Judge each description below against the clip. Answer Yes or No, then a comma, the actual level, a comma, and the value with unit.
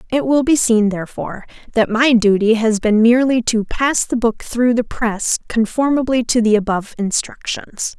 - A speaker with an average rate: Yes, average, 175 wpm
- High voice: Yes, high, 230 Hz